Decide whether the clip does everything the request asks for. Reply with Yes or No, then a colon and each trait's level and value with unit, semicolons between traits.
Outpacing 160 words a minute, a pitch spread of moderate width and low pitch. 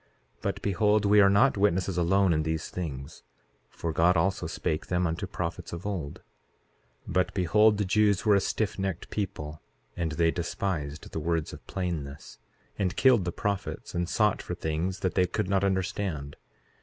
Yes: average, 170 wpm; average, 3.3 semitones; very low, 90 Hz